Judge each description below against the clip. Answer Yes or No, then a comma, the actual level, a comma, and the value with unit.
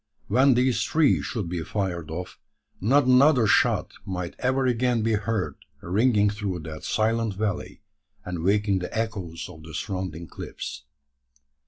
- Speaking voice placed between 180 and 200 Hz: No, low, 105 Hz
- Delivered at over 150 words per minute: No, average, 145 wpm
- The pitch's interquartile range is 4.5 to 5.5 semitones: Yes, average, 4.9 semitones